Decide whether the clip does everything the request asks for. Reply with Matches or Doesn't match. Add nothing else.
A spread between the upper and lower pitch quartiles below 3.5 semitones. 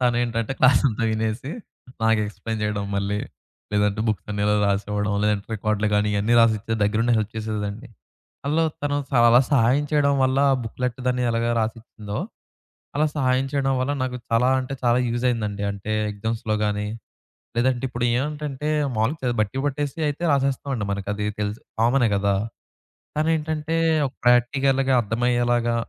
Doesn't match